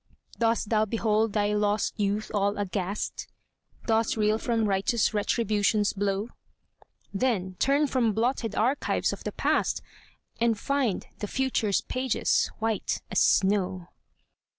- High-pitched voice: Yes, high, 215 Hz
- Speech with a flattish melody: Yes, narrow, 2.2 semitones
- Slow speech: Yes, slow, 125 wpm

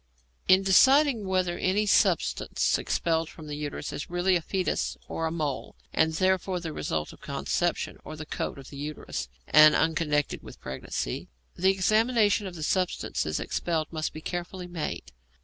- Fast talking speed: No, average, 165 wpm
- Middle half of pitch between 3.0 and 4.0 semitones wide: Yes, average, 3.6 semitones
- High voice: No, medium, 170 Hz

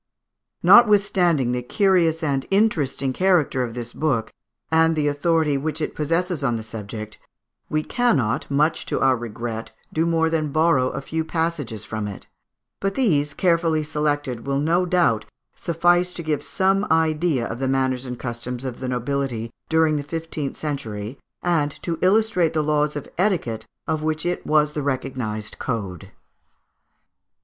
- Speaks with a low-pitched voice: No, medium, 150 Hz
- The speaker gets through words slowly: No, average, 155 wpm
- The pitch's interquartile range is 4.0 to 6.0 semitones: Yes, average, 4.7 semitones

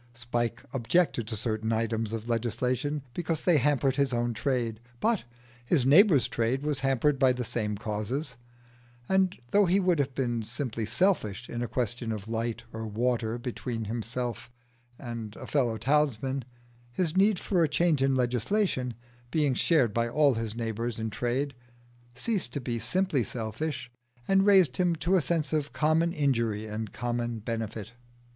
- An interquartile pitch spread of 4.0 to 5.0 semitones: Yes, average, 4.7 semitones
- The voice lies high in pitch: No, low, 125 Hz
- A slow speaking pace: No, average, 160 wpm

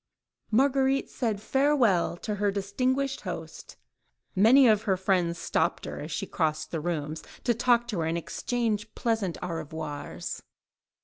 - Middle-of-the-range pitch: No, high, 205 Hz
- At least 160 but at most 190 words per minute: No, average, 145 wpm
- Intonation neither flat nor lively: No, wide, 6.2 semitones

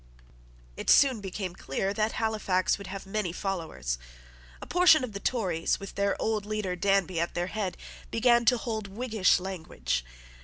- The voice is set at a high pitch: Yes, high, 200 Hz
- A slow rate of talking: No, average, 160 wpm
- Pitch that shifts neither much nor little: Yes, average, 3.2 semitones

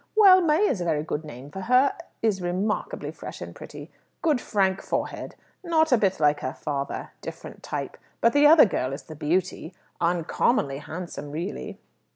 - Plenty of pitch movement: Yes, wide, 8.8 semitones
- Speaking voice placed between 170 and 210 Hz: Yes, medium, 185 Hz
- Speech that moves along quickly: No, average, 175 wpm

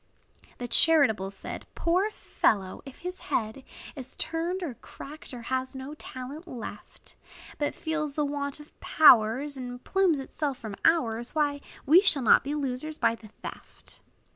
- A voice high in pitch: Yes, very high, 280 Hz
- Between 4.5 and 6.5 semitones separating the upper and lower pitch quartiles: No, average, 4.1 semitones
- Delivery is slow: No, average, 155 wpm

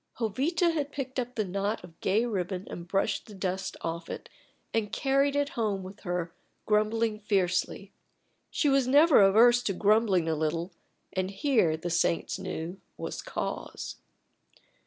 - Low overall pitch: No, high, 205 Hz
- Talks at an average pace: Yes, average, 155 wpm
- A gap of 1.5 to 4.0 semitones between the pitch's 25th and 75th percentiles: No, average, 5.1 semitones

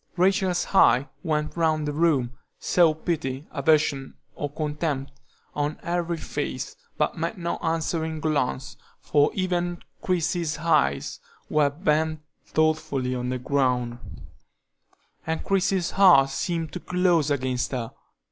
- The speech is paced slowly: Yes, slow, 120 wpm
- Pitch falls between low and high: Yes, medium, 155 Hz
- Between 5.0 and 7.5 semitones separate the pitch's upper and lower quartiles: No, average, 3.6 semitones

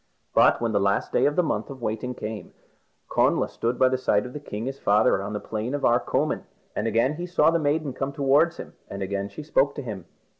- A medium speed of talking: No, fast, 235 wpm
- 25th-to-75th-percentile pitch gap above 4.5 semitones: Yes, average, 5.2 semitones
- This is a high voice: No, low, 125 Hz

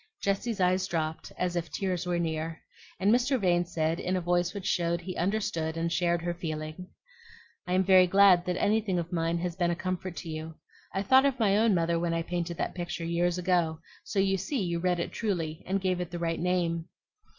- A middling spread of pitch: No, narrow, 2.0 semitones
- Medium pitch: Yes, medium, 175 Hz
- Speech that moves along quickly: Yes, fast, 215 wpm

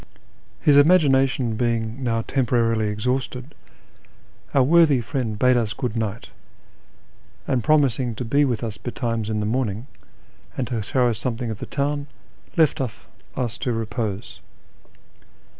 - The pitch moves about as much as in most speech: Yes, average, 3.0 semitones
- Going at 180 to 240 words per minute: No, slow, 135 wpm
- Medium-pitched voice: No, low, 120 Hz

